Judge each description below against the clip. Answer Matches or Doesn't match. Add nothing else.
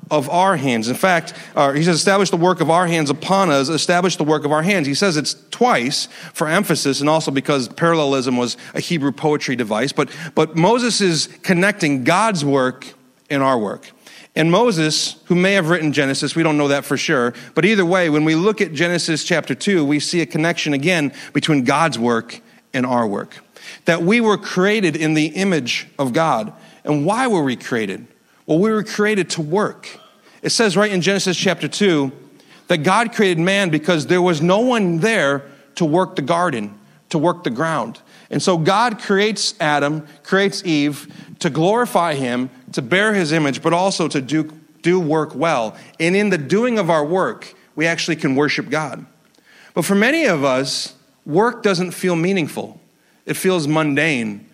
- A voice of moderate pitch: Matches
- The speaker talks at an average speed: Matches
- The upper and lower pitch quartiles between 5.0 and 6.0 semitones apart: Doesn't match